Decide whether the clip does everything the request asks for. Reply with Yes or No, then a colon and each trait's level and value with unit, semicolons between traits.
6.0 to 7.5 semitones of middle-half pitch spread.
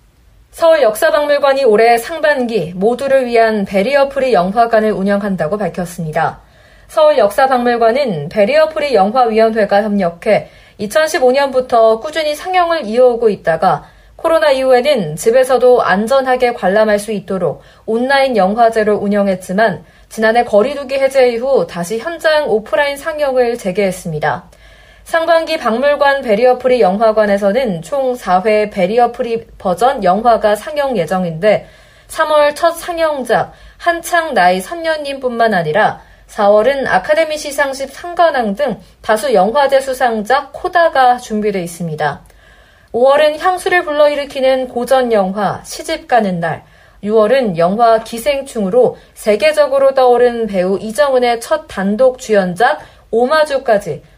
No: wide, 5.5 semitones